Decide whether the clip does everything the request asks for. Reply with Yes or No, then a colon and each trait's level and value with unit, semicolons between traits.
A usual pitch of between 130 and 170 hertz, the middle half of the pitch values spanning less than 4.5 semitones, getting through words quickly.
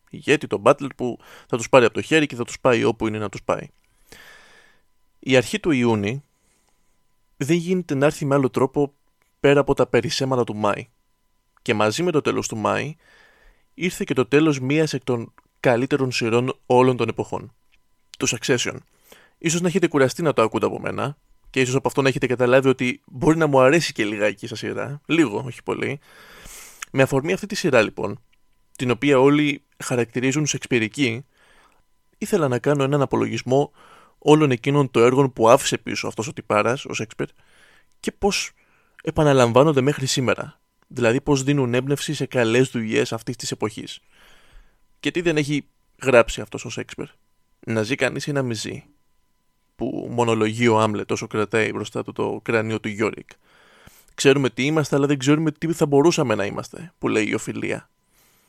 Yes: low, 135 Hz; average, 3.4 semitones; fast, 175 wpm